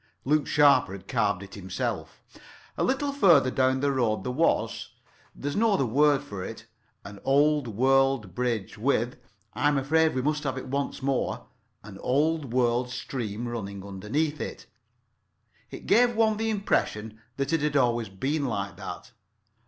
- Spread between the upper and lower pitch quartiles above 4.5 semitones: Yes, average, 5.2 semitones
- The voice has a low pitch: Yes, low, 130 Hz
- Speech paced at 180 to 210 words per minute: No, average, 145 wpm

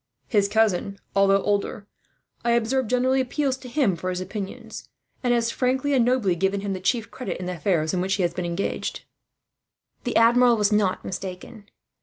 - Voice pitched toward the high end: Yes, high, 210 Hz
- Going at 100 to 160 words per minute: No, average, 185 wpm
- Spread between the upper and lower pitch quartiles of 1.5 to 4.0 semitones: No, average, 4.5 semitones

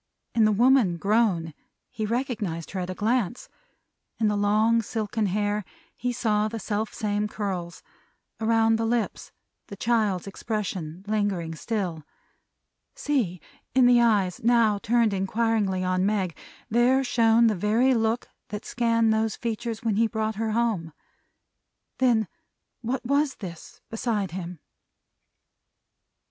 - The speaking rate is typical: No, slow, 130 wpm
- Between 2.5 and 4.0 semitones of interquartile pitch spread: Yes, average, 2.8 semitones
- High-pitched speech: Yes, high, 215 Hz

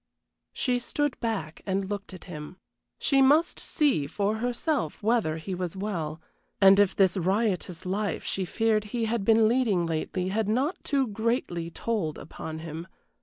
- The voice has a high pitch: Yes, high, 200 Hz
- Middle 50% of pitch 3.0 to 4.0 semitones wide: No, average, 4.8 semitones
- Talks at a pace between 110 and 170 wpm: Yes, average, 160 wpm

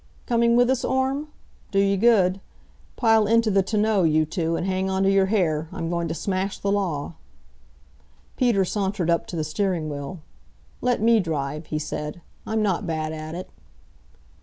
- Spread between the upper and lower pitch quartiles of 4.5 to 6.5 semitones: Yes, average, 4.9 semitones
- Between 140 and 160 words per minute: No, average, 175 wpm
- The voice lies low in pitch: No, high, 190 Hz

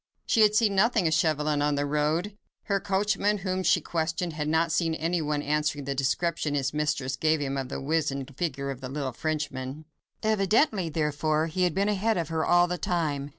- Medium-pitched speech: Yes, medium, 155 Hz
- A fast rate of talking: No, average, 195 wpm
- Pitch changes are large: No, average, 3.7 semitones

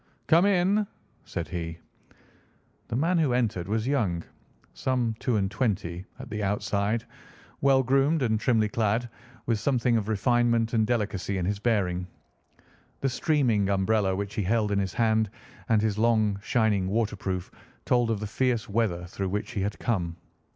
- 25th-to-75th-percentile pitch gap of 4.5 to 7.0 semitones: No, average, 3.4 semitones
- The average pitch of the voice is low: Yes, low, 110 Hz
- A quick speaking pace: No, average, 160 wpm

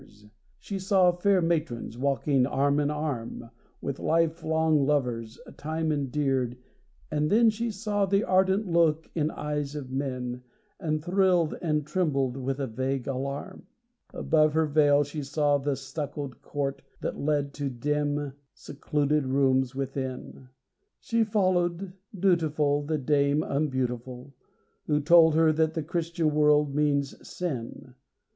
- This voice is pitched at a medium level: Yes, medium, 150 Hz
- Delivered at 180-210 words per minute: No, slow, 135 wpm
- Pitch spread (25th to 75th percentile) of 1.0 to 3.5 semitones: Yes, average, 3.0 semitones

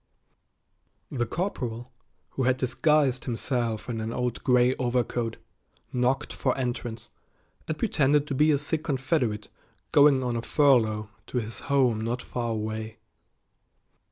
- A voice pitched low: Yes, low, 125 Hz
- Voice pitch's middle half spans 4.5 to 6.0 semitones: No, average, 3.2 semitones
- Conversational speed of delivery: No, slow, 130 wpm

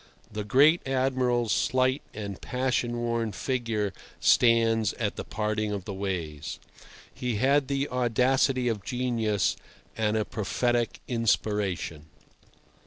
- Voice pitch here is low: Yes, low, 115 Hz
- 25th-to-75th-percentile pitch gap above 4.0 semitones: No, average, 3.3 semitones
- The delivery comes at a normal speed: No, slow, 115 wpm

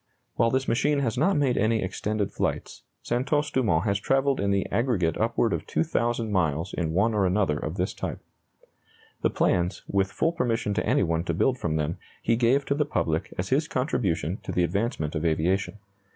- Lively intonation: Yes, wide, 6.2 semitones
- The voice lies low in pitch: Yes, low, 105 Hz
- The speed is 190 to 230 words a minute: Yes, average, 195 wpm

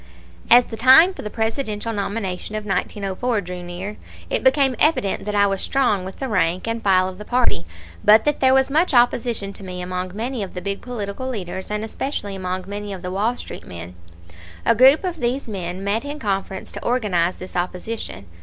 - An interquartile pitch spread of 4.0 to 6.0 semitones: Yes, average, 4.8 semitones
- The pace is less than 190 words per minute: No, average, 200 wpm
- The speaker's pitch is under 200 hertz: No, high, 210 Hz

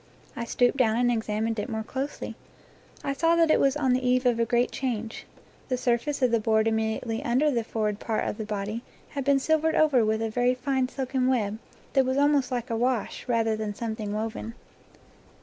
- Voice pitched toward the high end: Yes, high, 240 Hz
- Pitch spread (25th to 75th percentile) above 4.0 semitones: No, average, 3.0 semitones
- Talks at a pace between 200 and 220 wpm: Yes, fast, 205 wpm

